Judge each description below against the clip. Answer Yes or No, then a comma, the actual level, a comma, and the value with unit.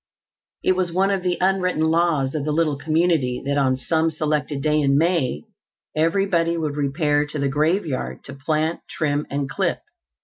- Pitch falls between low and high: Yes, medium, 155 Hz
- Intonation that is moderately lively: Yes, average, 3.0 semitones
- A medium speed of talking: Yes, average, 170 wpm